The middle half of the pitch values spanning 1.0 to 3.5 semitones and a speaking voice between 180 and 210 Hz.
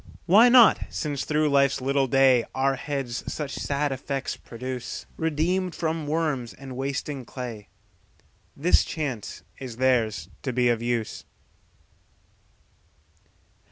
No: average, 3.2 semitones; low, 135 Hz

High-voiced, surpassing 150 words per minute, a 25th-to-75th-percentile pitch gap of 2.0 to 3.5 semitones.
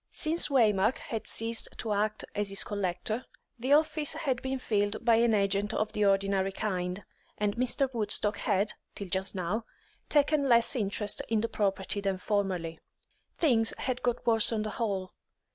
Yes: high, 215 Hz; average, 165 wpm; average, 3.2 semitones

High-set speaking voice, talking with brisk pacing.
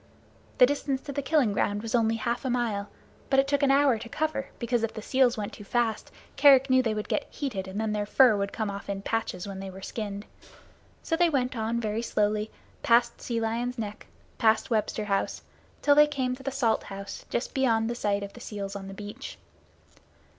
Yes: high, 230 Hz; fast, 220 wpm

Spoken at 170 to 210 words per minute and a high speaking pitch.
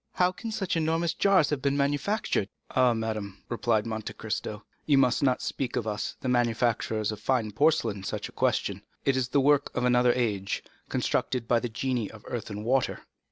No: average, 190 wpm; low, 125 Hz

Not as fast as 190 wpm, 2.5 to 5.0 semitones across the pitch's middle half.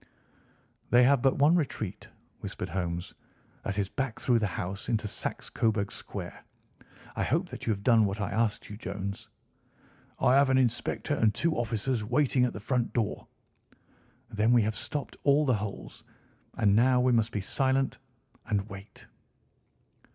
Yes: average, 165 wpm; average, 4.0 semitones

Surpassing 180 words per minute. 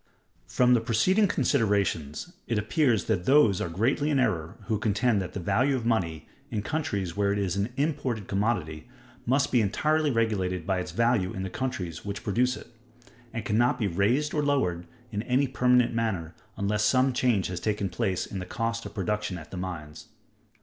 Yes: average, 190 wpm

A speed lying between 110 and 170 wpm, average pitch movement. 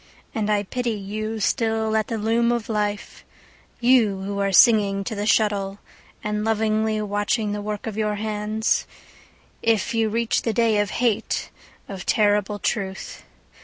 No: average, 155 wpm; narrow, 1.4 semitones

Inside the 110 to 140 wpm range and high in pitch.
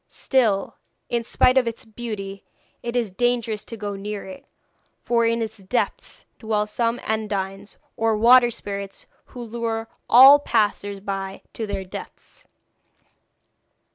Yes: slow, 135 wpm; high, 220 Hz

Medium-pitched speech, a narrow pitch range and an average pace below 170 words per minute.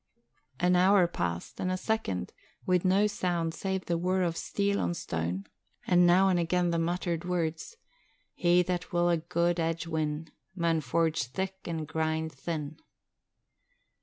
Yes: medium, 170 Hz; narrow, 2.2 semitones; average, 155 wpm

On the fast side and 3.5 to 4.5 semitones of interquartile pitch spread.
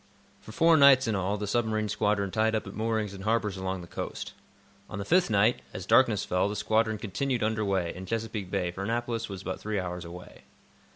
No: fast, 215 wpm; average, 2.8 semitones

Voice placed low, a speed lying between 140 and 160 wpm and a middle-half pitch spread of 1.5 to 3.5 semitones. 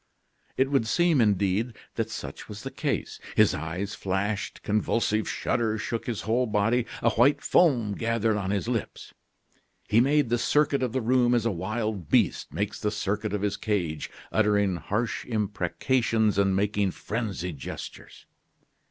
Yes: low, 110 Hz; average, 155 wpm; average, 2.8 semitones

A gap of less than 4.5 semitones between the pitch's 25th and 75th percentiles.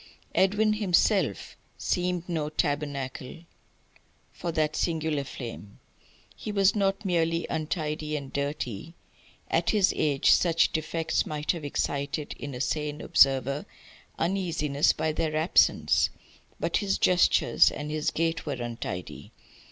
Yes: average, 3.2 semitones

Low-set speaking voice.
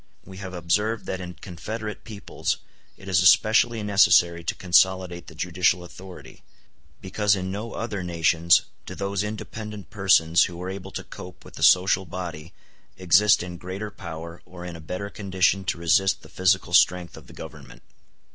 Yes: very low, 95 Hz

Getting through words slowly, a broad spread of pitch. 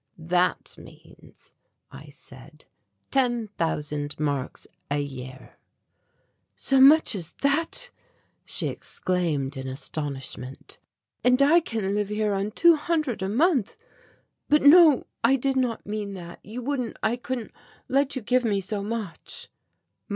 Yes: slow, 130 wpm; wide, 7.9 semitones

